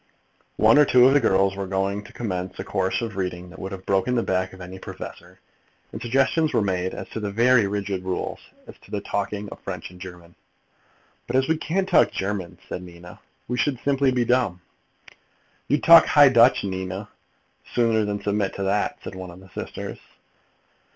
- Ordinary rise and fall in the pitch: Yes, average, 4.8 semitones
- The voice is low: Yes, low, 100 Hz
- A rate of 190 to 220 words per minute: Yes, average, 195 wpm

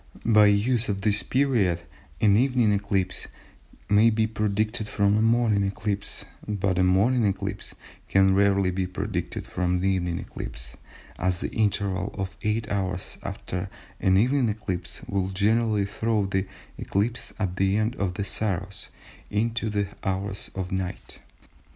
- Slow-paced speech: No, average, 145 wpm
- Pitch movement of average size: No, narrow, 2.3 semitones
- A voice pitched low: Yes, low, 100 Hz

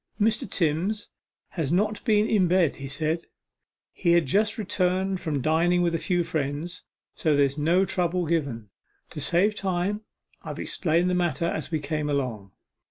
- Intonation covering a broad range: No, average, 3.6 semitones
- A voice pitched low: No, medium, 170 Hz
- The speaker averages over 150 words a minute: Yes, average, 165 wpm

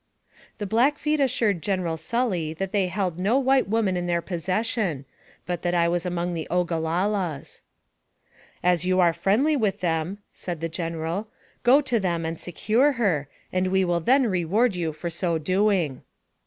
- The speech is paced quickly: No, average, 170 wpm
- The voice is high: No, medium, 180 Hz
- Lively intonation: No, average, 4.0 semitones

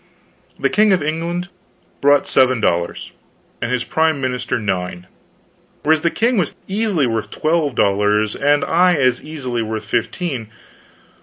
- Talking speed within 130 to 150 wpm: Yes, average, 140 wpm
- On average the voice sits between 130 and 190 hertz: Yes, medium, 140 Hz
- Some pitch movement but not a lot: No, wide, 6.6 semitones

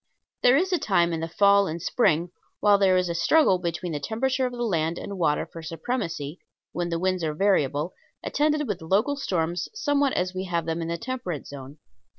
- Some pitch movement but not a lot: No, wide, 5.7 semitones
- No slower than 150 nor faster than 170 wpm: No, fast, 205 wpm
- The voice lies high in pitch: No, medium, 180 Hz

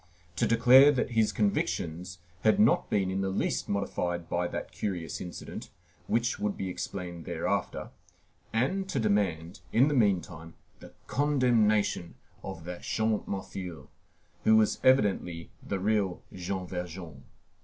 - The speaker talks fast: No, slow, 135 wpm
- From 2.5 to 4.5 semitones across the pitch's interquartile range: Yes, average, 4.2 semitones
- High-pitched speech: No, low, 100 Hz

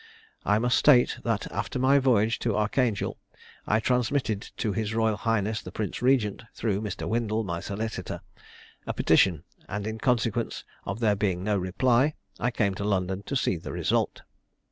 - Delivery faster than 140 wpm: Yes, average, 165 wpm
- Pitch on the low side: Yes, low, 110 Hz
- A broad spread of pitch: No, average, 3.0 semitones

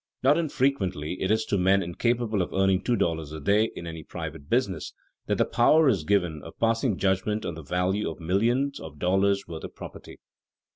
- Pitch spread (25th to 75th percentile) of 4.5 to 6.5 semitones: Yes, average, 4.8 semitones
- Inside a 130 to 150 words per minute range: No, average, 195 wpm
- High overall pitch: No, very low, 95 Hz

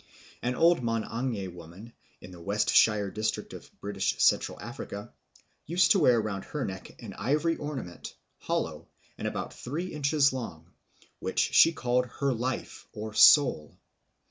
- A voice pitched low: Yes, low, 120 Hz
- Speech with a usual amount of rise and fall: No, wide, 6.0 semitones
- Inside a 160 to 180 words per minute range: No, average, 145 wpm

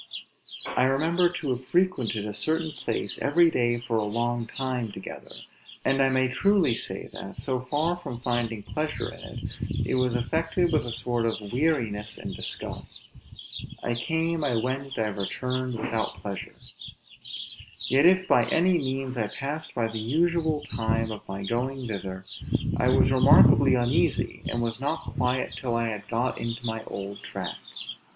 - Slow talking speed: No, average, 165 wpm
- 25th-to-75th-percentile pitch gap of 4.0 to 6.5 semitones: Yes, average, 4.5 semitones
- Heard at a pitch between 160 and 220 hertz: No, low, 125 Hz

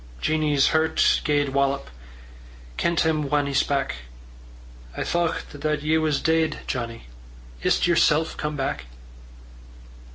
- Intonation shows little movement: Yes, narrow, 2.3 semitones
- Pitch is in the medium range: Yes, medium, 150 Hz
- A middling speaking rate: No, slow, 125 wpm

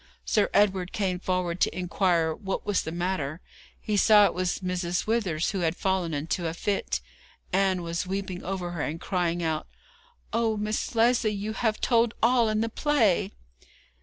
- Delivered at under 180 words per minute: Yes, average, 170 wpm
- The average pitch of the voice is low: No, high, 190 Hz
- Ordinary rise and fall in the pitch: Yes, average, 3.5 semitones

